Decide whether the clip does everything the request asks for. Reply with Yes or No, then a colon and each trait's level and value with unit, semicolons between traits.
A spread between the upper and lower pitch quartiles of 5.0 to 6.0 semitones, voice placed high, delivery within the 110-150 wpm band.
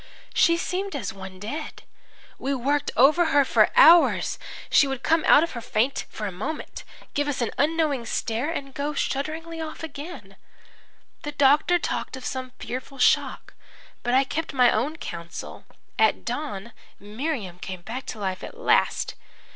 No: wide, 5.5 semitones; very high, 275 Hz; average, 165 wpm